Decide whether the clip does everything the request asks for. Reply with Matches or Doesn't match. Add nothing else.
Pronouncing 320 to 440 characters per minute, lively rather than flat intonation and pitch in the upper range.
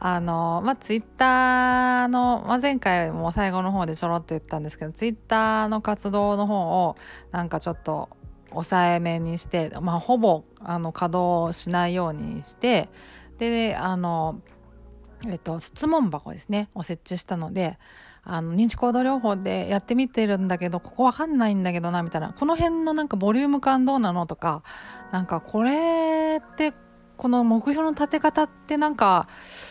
Matches